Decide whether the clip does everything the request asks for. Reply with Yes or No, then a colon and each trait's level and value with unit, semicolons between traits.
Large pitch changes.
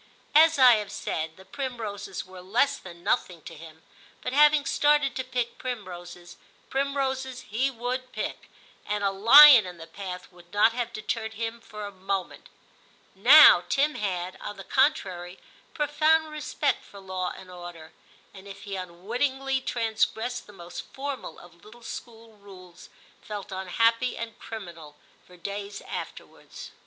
Yes: wide, 5.7 semitones